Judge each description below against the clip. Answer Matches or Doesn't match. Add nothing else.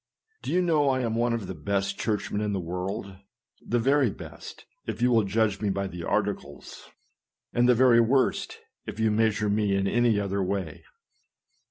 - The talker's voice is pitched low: Matches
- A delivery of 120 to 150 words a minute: Doesn't match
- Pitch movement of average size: Matches